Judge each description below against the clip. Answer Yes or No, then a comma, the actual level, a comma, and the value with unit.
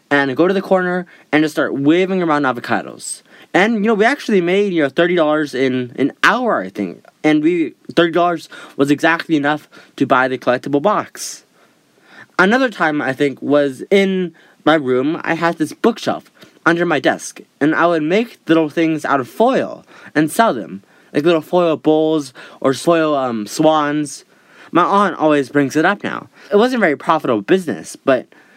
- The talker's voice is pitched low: No, medium, 160 Hz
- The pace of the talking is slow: No, average, 185 wpm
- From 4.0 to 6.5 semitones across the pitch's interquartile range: Yes, average, 4.3 semitones